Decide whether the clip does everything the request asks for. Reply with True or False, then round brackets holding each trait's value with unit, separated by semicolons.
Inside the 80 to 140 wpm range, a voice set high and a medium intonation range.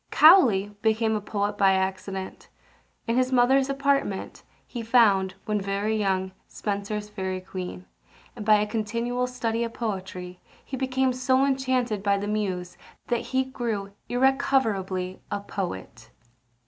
True (135 wpm; 215 Hz; 4.4 semitones)